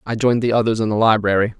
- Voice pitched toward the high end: No, low, 110 Hz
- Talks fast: Yes, fast, 265 wpm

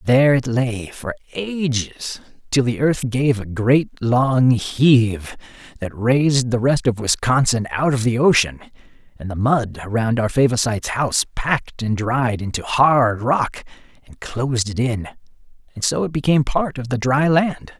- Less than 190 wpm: Yes, average, 165 wpm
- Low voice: Yes, low, 125 Hz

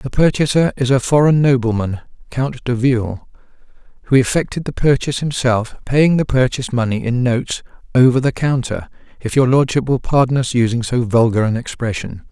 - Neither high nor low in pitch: No, low, 125 Hz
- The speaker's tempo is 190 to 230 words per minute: No, average, 165 wpm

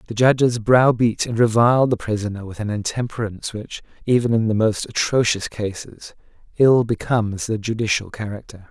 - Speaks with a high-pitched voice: No, low, 110 Hz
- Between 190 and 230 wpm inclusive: No, average, 150 wpm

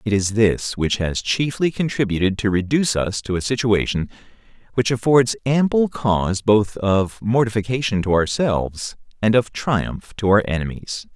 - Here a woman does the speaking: No, male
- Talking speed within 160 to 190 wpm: No, average, 150 wpm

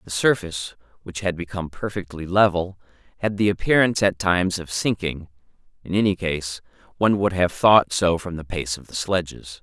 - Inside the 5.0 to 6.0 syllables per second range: Yes, 5.4 syllables/s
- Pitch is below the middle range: Yes, very low, 90 Hz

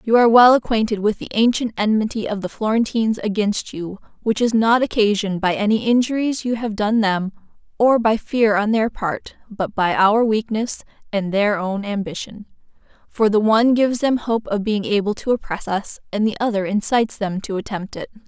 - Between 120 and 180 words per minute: No, average, 190 wpm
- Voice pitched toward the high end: Yes, high, 215 Hz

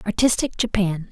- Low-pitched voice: No, high, 210 Hz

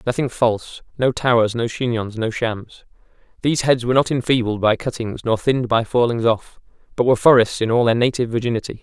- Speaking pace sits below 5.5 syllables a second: No, 6.0 syllables/s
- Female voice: No, male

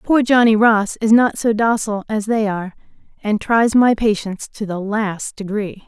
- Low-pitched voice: No, high, 215 Hz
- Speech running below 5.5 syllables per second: Yes, 4.8 syllables/s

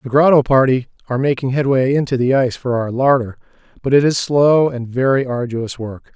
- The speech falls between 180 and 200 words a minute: Yes, average, 195 wpm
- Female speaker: No, male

